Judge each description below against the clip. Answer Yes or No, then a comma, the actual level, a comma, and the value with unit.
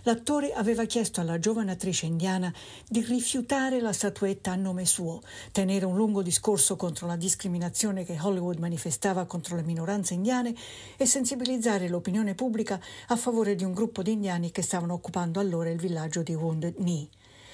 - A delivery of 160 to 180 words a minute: Yes, average, 165 wpm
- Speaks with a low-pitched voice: No, high, 190 Hz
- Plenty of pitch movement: No, average, 4.1 semitones